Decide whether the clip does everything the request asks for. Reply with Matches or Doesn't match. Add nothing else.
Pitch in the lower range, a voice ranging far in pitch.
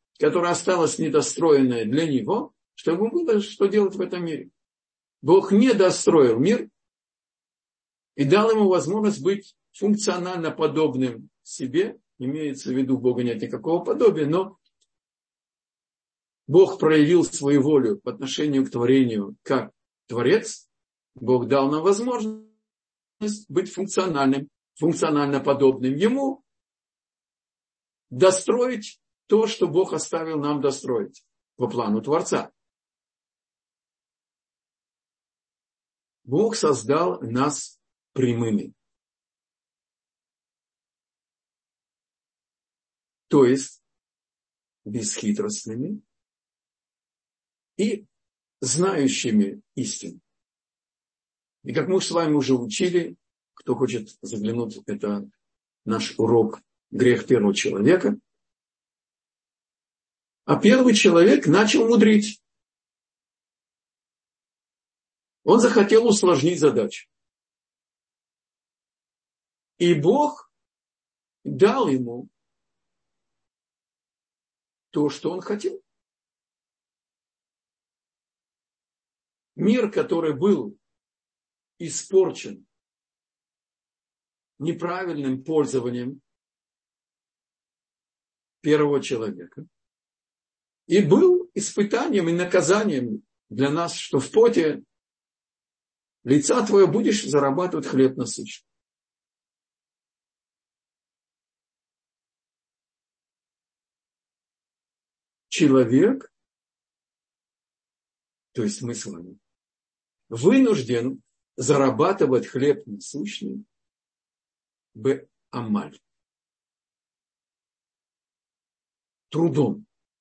Doesn't match